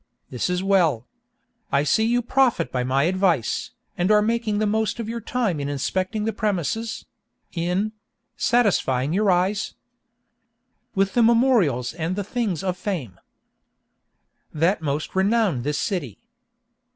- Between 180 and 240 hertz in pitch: Yes, high, 190 Hz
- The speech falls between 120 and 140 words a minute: Yes, slow, 135 wpm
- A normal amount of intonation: No, wide, 6.2 semitones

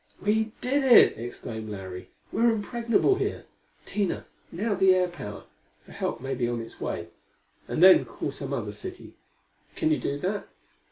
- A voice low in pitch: No, high, 190 Hz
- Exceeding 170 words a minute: No, average, 165 wpm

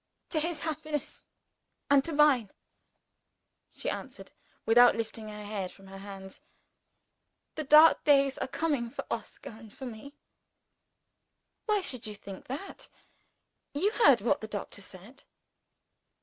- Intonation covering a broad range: Yes, wide, 6.1 semitones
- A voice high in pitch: Yes, high, 245 Hz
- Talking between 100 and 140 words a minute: Yes, slow, 135 wpm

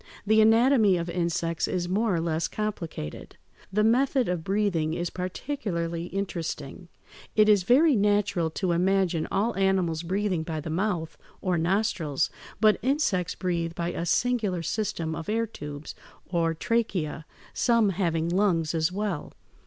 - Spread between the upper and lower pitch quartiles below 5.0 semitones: Yes, average, 4.2 semitones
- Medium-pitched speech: Yes, medium, 180 Hz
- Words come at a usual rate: Yes, average, 150 wpm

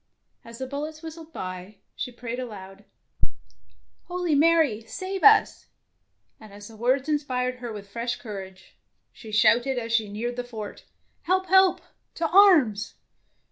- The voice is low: No, high, 245 Hz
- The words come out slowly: No, average, 160 wpm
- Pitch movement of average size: No, wide, 6.6 semitones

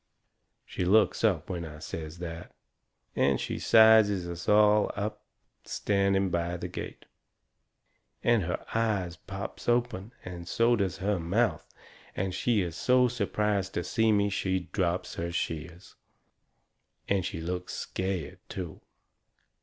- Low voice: Yes, very low, 95 Hz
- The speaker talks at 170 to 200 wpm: No, slow, 135 wpm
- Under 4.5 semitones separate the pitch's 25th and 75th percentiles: Yes, average, 3.5 semitones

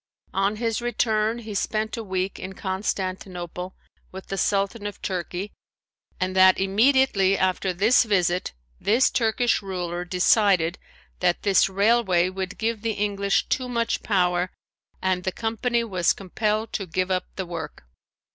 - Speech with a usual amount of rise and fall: Yes, average, 3.0 semitones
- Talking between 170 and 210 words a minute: No, average, 145 wpm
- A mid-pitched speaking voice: No, high, 195 Hz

